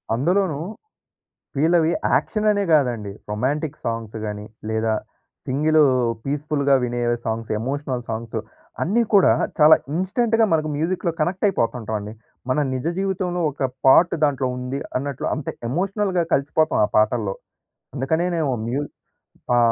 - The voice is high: No, medium, 145 Hz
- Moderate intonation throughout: No, wide, 6.1 semitones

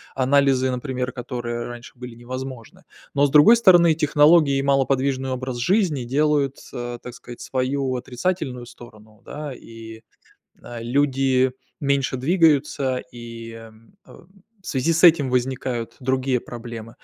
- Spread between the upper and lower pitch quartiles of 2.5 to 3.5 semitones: Yes, average, 2.9 semitones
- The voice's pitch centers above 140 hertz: No, low, 130 Hz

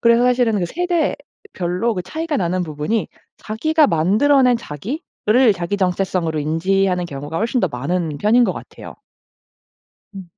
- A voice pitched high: Yes, high, 195 Hz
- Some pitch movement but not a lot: No, wide, 6.1 semitones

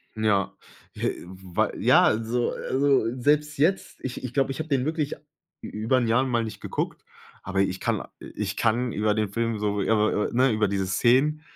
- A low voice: Yes, low, 115 Hz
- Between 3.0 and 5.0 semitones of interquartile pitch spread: Yes, average, 4.1 semitones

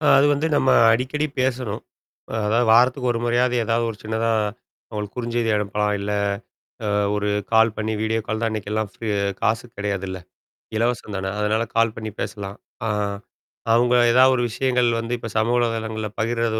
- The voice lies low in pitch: Yes, low, 115 Hz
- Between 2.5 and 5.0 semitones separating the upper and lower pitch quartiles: No, narrow, 2.0 semitones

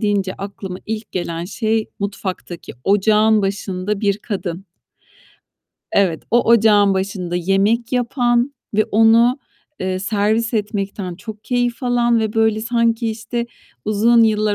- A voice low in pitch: No, high, 215 Hz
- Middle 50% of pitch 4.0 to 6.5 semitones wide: No, average, 2.8 semitones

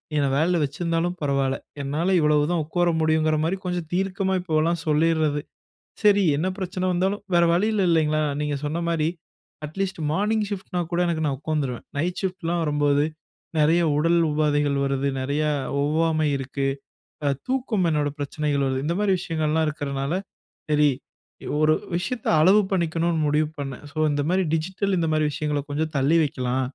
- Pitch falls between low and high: Yes, medium, 155 Hz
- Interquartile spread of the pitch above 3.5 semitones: No, average, 3.2 semitones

